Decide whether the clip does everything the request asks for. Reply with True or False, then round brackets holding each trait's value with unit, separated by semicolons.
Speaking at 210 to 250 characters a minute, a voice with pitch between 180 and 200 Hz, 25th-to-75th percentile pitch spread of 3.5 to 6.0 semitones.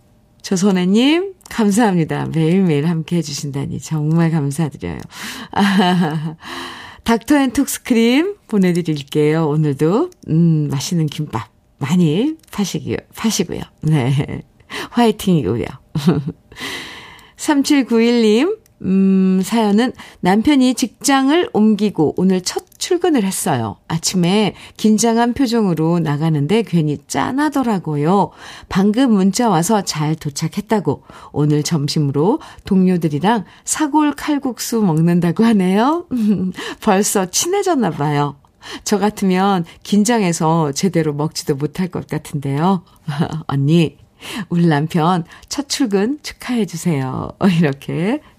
False (245 characters per minute; 185 Hz; 6.6 semitones)